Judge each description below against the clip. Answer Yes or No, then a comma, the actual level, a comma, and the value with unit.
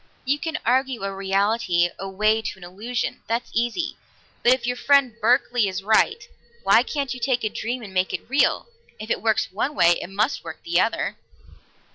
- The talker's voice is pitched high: Yes, high, 230 Hz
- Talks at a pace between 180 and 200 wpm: Yes, average, 190 wpm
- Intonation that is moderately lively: Yes, average, 4.6 semitones